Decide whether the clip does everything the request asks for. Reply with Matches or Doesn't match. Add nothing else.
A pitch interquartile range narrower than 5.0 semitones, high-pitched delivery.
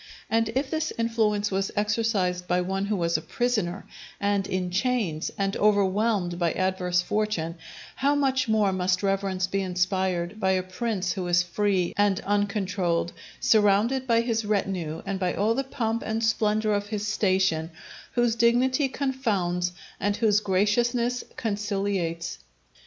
Matches